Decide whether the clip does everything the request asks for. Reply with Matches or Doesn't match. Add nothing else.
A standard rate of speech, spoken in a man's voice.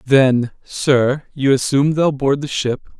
Matches